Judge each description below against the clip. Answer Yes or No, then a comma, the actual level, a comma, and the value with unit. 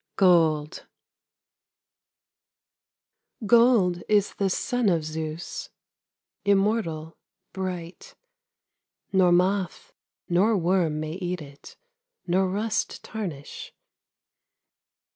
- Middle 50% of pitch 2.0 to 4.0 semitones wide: Yes, average, 3.6 semitones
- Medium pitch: Yes, medium, 180 Hz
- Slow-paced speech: Yes, slow, 75 wpm